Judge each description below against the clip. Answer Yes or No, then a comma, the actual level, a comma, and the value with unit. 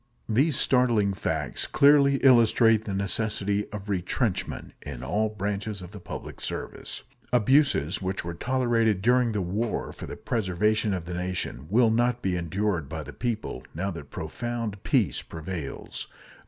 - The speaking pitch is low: Yes, low, 105 Hz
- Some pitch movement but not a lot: Yes, average, 4.6 semitones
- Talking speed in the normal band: Yes, average, 150 wpm